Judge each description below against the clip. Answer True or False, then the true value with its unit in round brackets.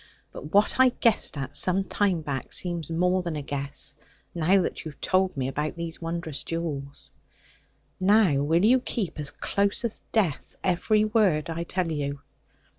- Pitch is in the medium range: True (170 Hz)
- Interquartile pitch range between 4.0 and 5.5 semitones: True (4.6 semitones)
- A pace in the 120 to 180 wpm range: True (170 wpm)